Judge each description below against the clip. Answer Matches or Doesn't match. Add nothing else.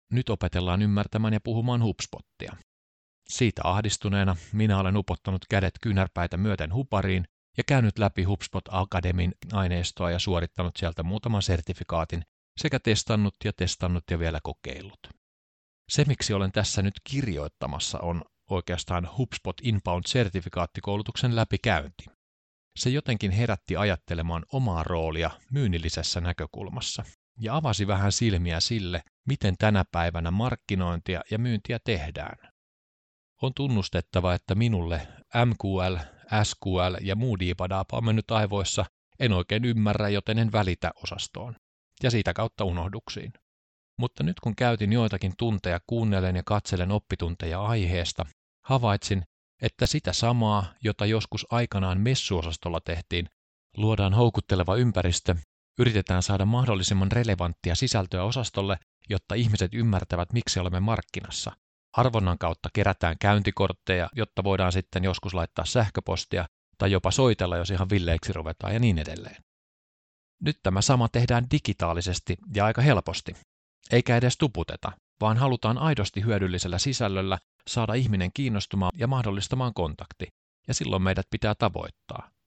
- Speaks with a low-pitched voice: Matches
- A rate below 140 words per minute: Matches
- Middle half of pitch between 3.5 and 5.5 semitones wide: Matches